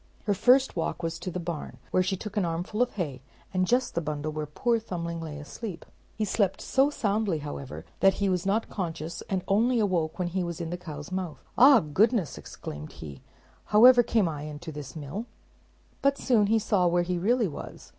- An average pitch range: Yes, average, 4.8 semitones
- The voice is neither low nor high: Yes, medium, 180 Hz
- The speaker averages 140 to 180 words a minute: No, fast, 205 wpm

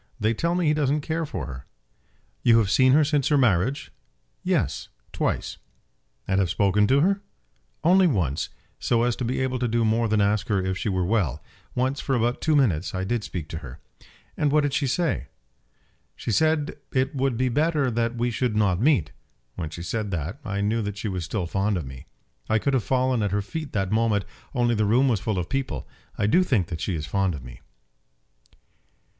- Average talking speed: No, fast, 210 wpm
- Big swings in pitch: Yes, wide, 6.0 semitones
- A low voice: Yes, low, 115 Hz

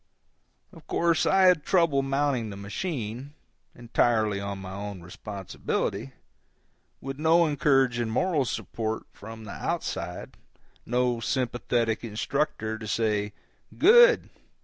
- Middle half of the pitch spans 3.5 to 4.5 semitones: No, wide, 5.4 semitones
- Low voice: Yes, low, 120 Hz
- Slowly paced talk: Yes, slow, 110 wpm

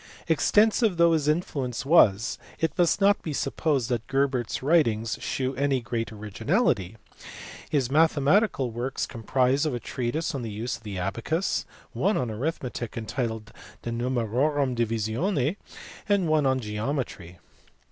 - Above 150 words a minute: No, average, 140 wpm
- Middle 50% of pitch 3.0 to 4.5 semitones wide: No, average, 5.2 semitones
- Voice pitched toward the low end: Yes, low, 130 Hz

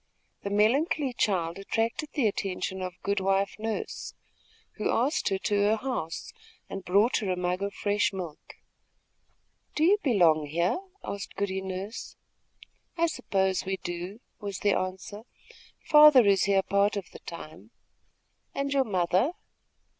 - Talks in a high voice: Yes, high, 200 Hz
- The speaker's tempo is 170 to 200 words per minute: No, average, 145 wpm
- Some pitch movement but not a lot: Yes, average, 3.4 semitones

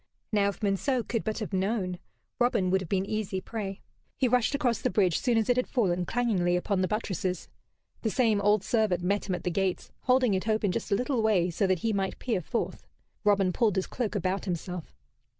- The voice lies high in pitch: Yes, high, 200 Hz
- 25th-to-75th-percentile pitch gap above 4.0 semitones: No, average, 3.4 semitones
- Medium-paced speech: No, fast, 215 wpm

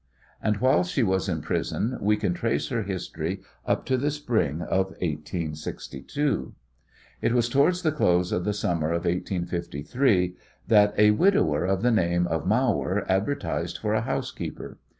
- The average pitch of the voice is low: Yes, low, 100 Hz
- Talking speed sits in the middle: Yes, average, 155 wpm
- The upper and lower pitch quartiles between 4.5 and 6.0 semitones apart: Yes, average, 5.3 semitones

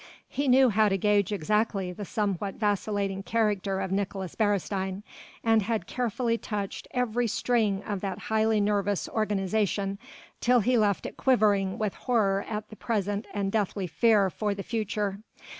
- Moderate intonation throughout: No, narrow, 2.0 semitones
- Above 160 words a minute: No, average, 155 wpm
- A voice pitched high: Yes, high, 205 Hz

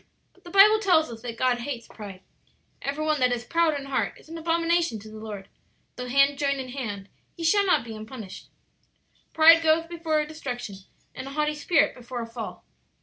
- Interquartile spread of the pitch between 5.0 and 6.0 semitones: Yes, wide, 5.6 semitones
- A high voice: Yes, very high, 275 Hz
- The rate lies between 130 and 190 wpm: No, average, 200 wpm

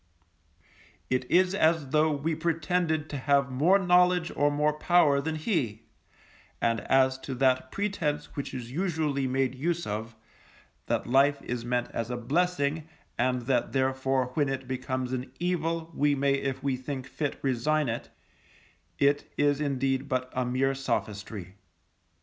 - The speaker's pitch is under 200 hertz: Yes, medium, 140 Hz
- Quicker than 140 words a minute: Yes, average, 150 wpm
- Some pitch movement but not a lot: Yes, average, 3.4 semitones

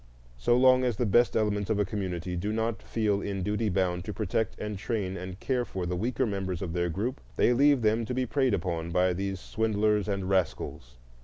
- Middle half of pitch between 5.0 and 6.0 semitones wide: No, average, 3.5 semitones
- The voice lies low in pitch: Yes, low, 105 Hz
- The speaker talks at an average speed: No, fast, 215 wpm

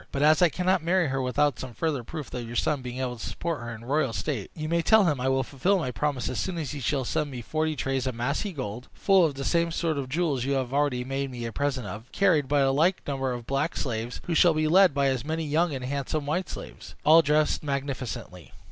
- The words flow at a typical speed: No, fast, 260 wpm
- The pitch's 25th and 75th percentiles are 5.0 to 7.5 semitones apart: No, average, 3.7 semitones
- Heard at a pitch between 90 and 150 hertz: Yes, medium, 140 Hz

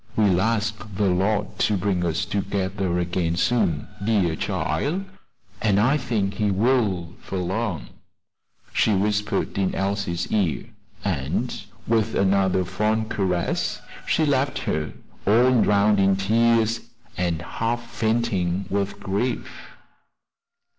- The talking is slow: Yes, slow, 120 wpm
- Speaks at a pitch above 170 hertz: No, low, 100 Hz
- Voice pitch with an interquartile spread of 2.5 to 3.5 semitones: Yes, average, 3.2 semitones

